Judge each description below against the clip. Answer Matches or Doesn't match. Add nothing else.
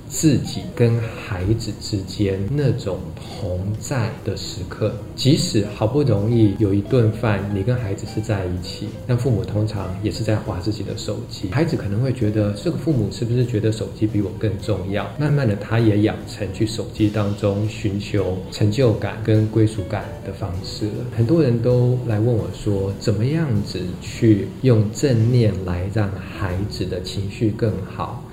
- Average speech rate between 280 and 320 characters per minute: Doesn't match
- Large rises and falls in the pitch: Doesn't match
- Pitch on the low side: Matches